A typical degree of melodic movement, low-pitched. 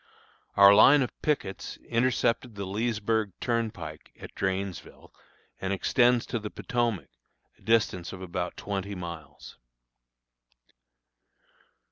Yes: average, 3.6 semitones; low, 105 Hz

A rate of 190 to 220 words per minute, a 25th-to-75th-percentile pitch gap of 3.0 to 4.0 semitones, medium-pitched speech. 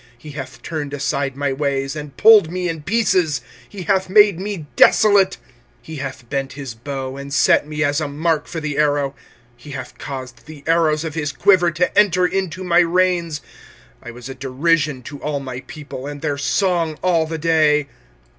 Yes: average, 200 wpm; average, 3.7 semitones; medium, 150 Hz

